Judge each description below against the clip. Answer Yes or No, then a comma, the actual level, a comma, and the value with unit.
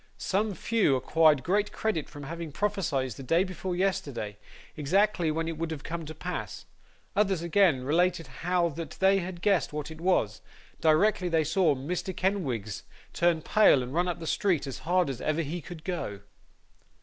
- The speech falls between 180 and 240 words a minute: No, average, 170 wpm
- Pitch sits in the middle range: Yes, medium, 165 Hz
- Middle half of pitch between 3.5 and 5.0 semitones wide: Yes, average, 4.0 semitones